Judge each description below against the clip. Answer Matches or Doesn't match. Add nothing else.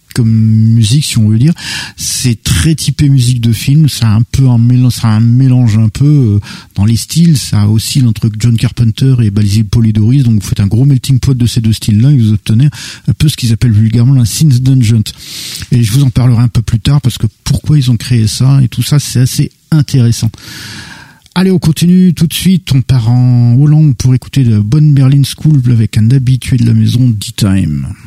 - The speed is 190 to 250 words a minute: Matches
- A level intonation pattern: Doesn't match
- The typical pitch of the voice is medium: Doesn't match